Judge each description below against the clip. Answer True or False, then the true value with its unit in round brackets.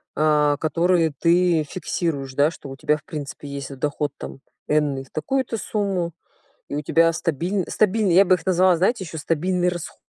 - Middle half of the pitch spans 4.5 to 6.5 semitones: False (3.6 semitones)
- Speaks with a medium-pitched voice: True (165 Hz)